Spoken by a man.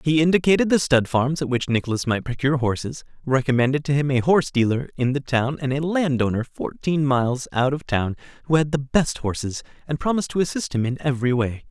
Yes: male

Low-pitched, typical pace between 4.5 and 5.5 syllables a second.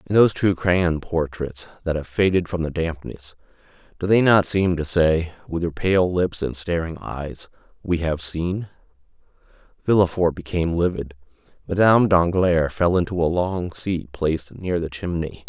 Yes: very low, 85 Hz; 4.6 syllables/s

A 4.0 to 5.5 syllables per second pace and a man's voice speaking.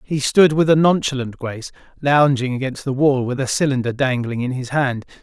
Yes: 5.4 syllables/s; male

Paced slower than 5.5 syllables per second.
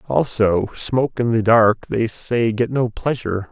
Yes: 4.3 syllables/s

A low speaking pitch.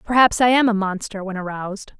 No: high, 210 Hz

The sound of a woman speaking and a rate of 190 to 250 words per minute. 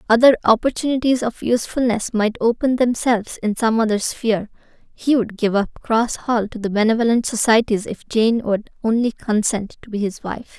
No: female; average, 170 wpm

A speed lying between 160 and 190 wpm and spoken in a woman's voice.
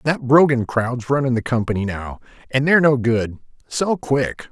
No: average, 175 wpm; male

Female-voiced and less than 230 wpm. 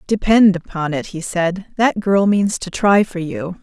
Yes: female; average, 200 wpm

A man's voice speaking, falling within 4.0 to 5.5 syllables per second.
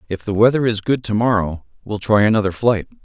No: male; 5.9 syllables/s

